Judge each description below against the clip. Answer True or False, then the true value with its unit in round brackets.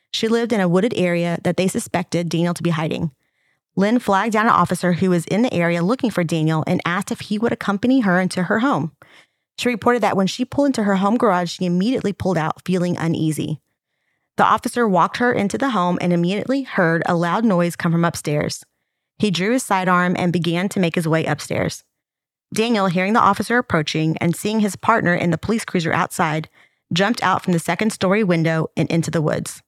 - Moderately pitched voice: True (180 Hz)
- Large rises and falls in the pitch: False (4.0 semitones)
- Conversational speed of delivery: False (210 wpm)